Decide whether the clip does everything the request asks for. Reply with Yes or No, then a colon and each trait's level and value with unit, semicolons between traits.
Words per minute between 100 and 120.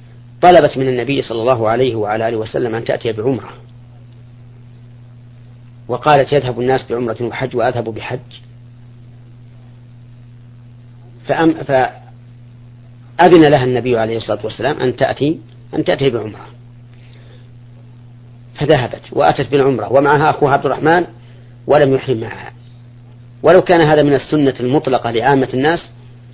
Yes: average, 110 wpm